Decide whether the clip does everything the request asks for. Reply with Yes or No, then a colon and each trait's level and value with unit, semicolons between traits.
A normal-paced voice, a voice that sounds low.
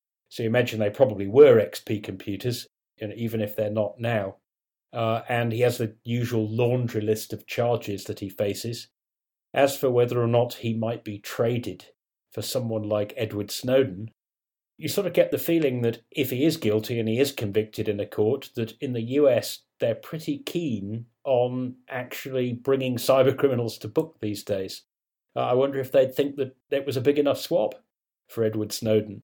Yes: average, 190 wpm; low, 120 Hz